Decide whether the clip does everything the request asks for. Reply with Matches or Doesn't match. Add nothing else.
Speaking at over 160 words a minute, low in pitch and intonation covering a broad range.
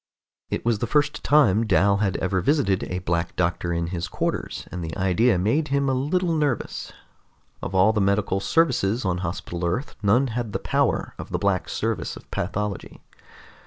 Matches